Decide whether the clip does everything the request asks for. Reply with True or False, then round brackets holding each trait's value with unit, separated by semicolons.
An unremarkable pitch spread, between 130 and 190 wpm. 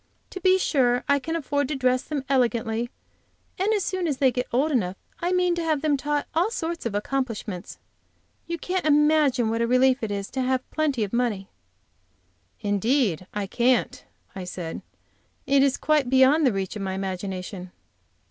False (5.8 semitones; 180 wpm)